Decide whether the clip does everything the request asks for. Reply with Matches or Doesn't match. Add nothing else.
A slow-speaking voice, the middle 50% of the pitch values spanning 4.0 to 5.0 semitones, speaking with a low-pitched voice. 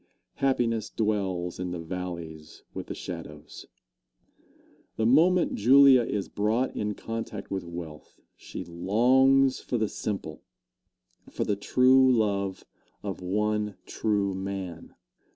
Matches